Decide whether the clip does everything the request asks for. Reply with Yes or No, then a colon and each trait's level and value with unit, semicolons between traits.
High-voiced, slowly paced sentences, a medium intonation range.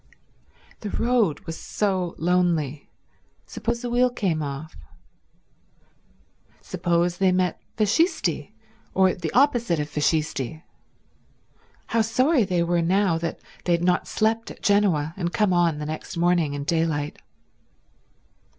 No: medium, 175 Hz; slow, 125 wpm; average, 4.7 semitones